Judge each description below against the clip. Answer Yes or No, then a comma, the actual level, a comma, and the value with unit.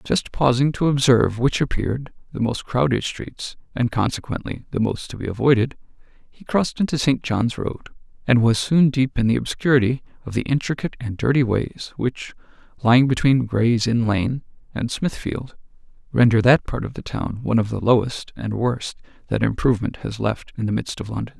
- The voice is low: Yes, low, 125 Hz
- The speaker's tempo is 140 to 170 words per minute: No, average, 180 wpm